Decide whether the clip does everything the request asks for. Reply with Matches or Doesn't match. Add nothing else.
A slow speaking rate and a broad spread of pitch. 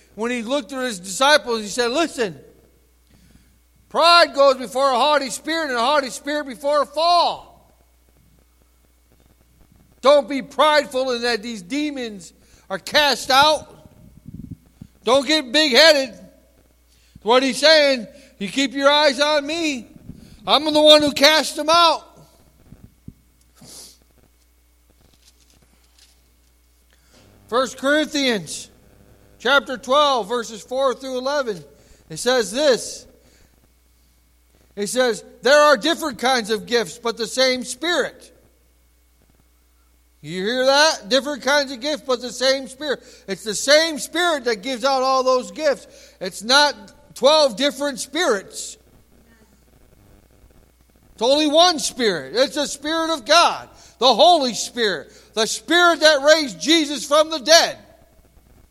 Matches